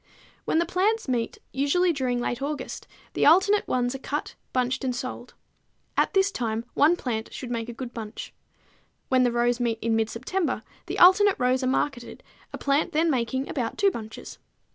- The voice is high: Yes, very high, 255 Hz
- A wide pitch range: No, average, 4.8 semitones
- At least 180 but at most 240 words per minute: Yes, average, 185 wpm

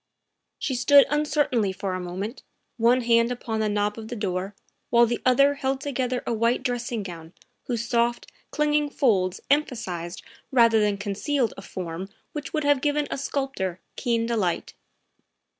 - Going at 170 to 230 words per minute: No, average, 160 wpm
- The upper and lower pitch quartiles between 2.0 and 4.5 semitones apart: No, average, 5.0 semitones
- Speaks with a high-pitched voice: Yes, high, 235 Hz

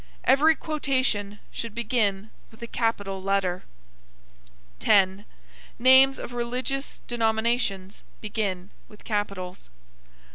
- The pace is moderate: No, slow, 95 wpm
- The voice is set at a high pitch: Yes, high, 220 Hz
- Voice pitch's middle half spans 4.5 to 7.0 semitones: No, average, 3.7 semitones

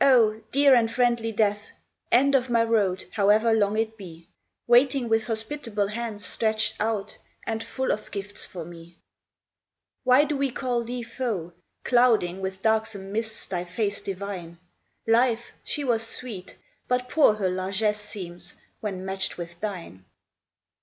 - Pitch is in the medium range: No, high, 220 Hz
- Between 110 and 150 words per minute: Yes, average, 145 wpm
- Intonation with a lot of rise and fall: No, average, 3.6 semitones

